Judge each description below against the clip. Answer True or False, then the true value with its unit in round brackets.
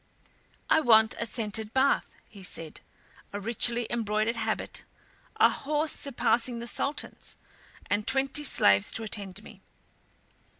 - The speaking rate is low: True (125 wpm)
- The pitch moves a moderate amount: True (3.8 semitones)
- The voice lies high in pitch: True (230 Hz)